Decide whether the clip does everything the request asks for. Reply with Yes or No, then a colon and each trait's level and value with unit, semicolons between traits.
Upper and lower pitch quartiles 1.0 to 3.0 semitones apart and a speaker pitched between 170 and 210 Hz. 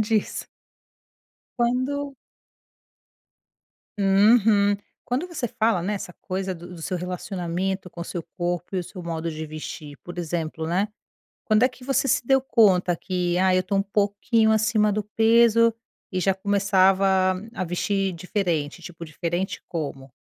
No: average, 3.6 semitones; high, 190 Hz